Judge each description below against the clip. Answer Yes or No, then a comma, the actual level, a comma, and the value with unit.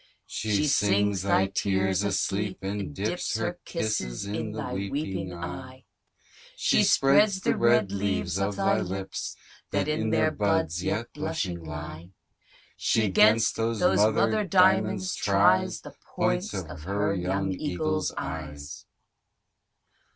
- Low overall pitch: Yes, low, 100 Hz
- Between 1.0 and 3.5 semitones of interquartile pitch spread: Yes, average, 3.2 semitones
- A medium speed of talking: No, slow, 120 wpm